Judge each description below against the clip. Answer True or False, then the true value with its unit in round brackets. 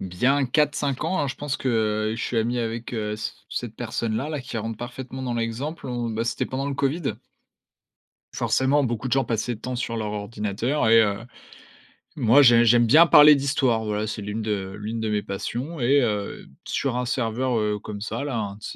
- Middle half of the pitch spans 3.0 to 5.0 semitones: True (3.6 semitones)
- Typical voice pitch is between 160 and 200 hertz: False (120 Hz)